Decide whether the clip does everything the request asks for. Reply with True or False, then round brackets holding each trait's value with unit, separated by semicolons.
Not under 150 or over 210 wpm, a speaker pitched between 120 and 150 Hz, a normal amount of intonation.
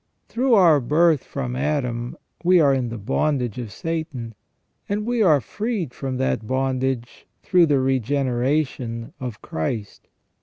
False (140 wpm; 135 Hz; 4.6 semitones)